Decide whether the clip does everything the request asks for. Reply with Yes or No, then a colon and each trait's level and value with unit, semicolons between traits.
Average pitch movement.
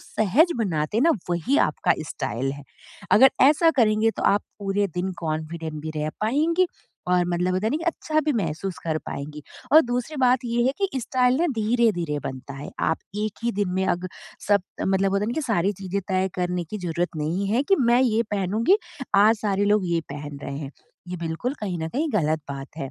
No: wide, 6.2 semitones